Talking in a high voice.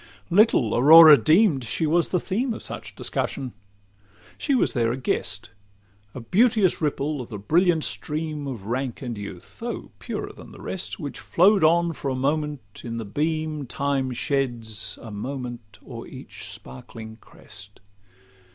No: medium, 140 Hz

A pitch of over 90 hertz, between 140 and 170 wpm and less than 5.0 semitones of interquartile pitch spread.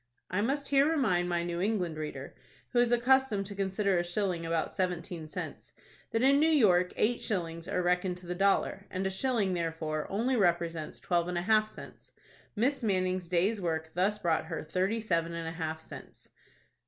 No: medium, 185 Hz; average, 190 wpm; average, 4.1 semitones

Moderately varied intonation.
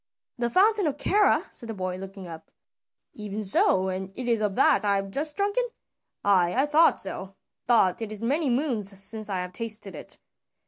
No: wide, 5.8 semitones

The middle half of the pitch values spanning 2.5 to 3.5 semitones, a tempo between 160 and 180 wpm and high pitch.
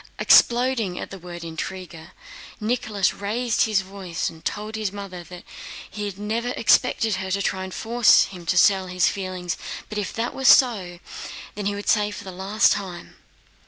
Yes: average, 2.8 semitones; average, 165 wpm; high, 200 Hz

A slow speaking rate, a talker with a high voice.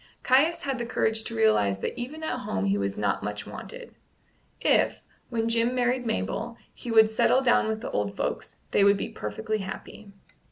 No: average, 190 wpm; high, 220 Hz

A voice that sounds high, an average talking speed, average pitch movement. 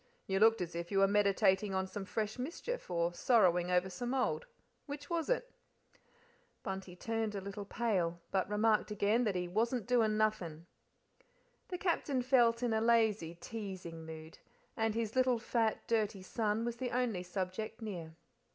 Yes: high, 215 Hz; average, 160 wpm; average, 3.9 semitones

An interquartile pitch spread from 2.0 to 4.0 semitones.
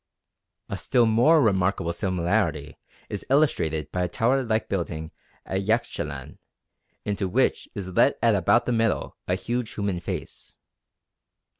No: average, 4.6 semitones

